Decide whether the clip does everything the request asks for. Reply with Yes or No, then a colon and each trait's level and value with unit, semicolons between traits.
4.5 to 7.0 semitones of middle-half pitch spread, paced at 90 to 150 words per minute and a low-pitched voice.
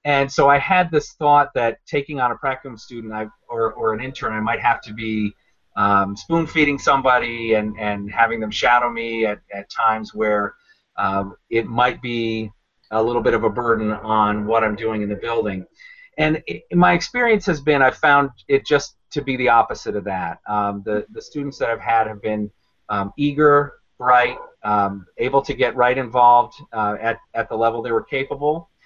No: average, 4.8 semitones; average, 200 wpm; low, 115 Hz